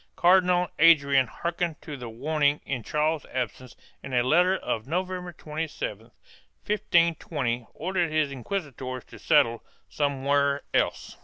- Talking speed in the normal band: No, slow, 130 wpm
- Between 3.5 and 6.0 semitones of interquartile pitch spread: Yes, average, 4.7 semitones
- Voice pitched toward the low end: No, medium, 150 Hz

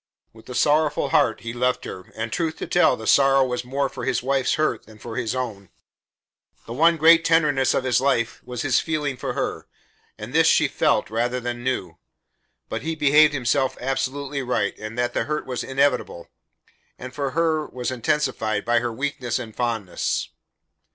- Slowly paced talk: No, average, 185 wpm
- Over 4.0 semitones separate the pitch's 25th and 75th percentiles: No, average, 3.2 semitones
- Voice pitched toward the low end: Yes, low, 130 Hz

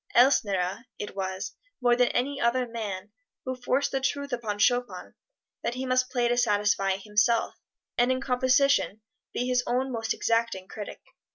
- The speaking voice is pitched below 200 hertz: No, high, 240 Hz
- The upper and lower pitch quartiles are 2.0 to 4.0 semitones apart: Yes, average, 3.5 semitones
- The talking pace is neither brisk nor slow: Yes, average, 160 wpm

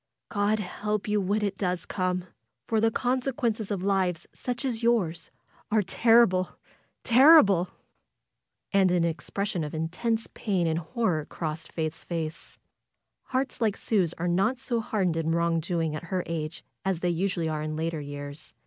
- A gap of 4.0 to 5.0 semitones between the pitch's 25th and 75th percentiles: Yes, average, 4.7 semitones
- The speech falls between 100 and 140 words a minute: No, average, 160 wpm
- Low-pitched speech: No, medium, 185 Hz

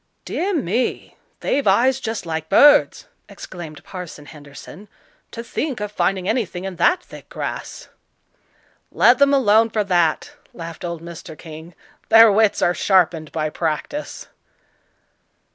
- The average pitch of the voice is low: No, high, 190 Hz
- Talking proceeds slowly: Yes, slow, 130 wpm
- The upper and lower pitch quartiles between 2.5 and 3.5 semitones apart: No, wide, 5.6 semitones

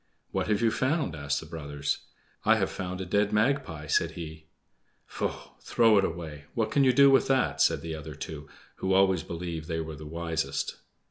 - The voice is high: No, very low, 85 Hz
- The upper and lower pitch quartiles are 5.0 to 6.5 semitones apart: Yes, wide, 5.5 semitones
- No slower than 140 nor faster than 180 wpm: No, average, 195 wpm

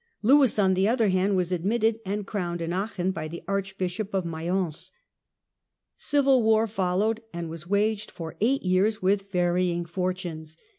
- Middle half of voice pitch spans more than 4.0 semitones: No, average, 3.4 semitones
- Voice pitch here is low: No, high, 190 Hz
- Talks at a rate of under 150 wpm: No, average, 155 wpm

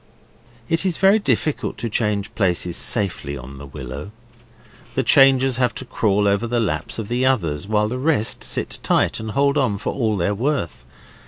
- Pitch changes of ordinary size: No, wide, 6.0 semitones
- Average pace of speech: Yes, average, 180 wpm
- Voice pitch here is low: Yes, low, 110 Hz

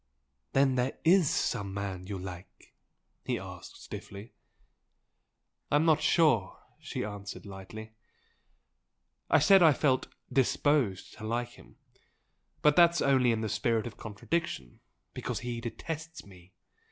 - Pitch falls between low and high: No, low, 120 Hz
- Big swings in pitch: Yes, wide, 6.7 semitones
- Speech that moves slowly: Yes, slow, 130 wpm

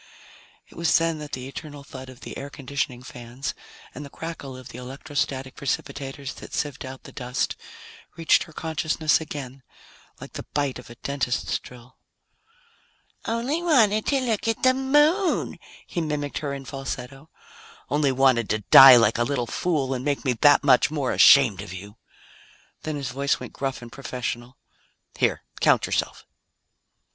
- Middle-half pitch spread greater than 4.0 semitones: No, average, 3.5 semitones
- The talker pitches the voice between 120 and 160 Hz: Yes, medium, 140 Hz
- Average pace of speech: Yes, average, 165 wpm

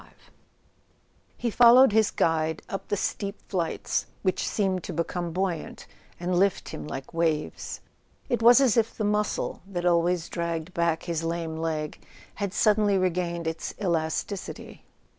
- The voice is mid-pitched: Yes, medium, 175 Hz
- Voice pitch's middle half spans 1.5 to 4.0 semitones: Yes, average, 3.6 semitones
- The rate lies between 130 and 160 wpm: Yes, average, 150 wpm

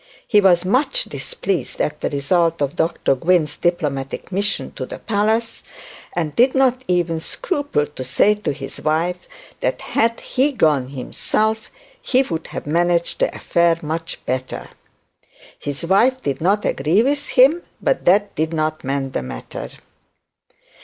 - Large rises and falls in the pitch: Yes, wide, 6.5 semitones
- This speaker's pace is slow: No, average, 150 wpm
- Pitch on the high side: No, medium, 175 Hz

